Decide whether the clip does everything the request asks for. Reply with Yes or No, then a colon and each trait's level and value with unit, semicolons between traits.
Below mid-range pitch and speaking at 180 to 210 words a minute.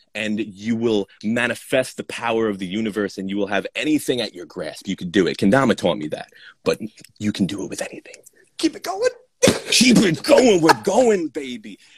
Yes: low, 120 Hz; fast, 205 wpm